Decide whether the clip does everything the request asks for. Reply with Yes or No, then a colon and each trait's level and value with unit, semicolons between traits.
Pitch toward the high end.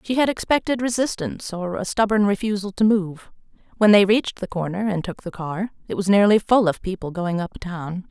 Yes: high, 200 Hz